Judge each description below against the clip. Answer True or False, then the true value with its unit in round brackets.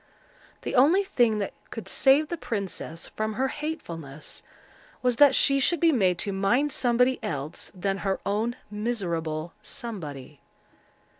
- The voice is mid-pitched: False (215 Hz)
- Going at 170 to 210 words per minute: False (140 wpm)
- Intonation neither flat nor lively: False (7.3 semitones)